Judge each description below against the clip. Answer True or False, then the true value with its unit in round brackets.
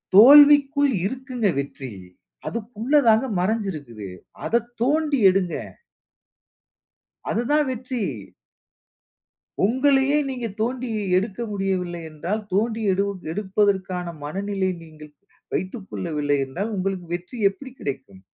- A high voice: True (205 Hz)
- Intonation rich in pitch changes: True (5.8 semitones)